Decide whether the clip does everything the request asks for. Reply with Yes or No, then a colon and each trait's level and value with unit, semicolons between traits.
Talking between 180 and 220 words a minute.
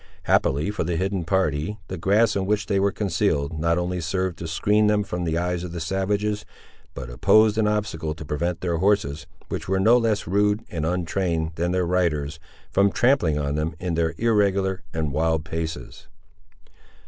Yes: average, 185 wpm